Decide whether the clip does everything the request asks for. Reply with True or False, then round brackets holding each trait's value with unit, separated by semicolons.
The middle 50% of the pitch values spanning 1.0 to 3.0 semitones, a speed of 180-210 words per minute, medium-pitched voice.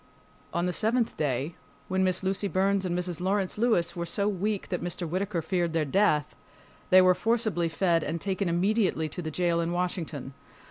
True (2.6 semitones; 185 wpm; 180 Hz)